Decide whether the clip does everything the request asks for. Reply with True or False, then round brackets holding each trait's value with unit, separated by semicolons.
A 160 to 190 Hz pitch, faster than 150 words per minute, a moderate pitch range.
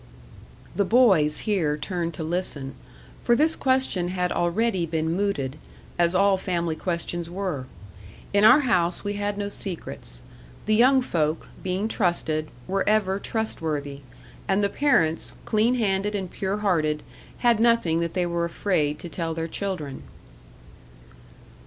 False (185 Hz; 140 wpm; 4.1 semitones)